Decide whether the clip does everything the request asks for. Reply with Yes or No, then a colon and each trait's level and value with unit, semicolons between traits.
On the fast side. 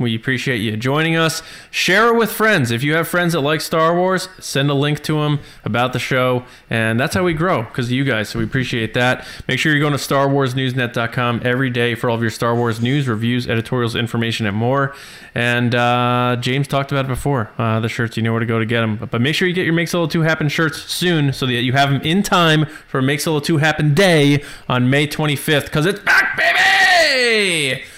Yes: fast, 235 wpm